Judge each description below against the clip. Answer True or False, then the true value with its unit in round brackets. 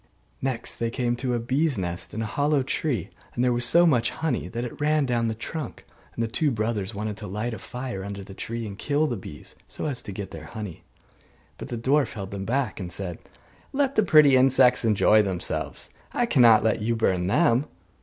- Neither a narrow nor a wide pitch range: True (4.5 semitones)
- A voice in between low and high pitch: False (115 Hz)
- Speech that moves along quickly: True (215 wpm)